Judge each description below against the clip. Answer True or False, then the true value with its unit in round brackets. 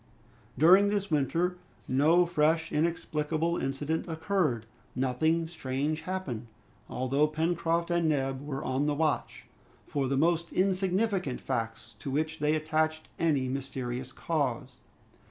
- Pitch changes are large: False (3.8 semitones)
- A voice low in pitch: False (155 Hz)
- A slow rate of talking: True (120 wpm)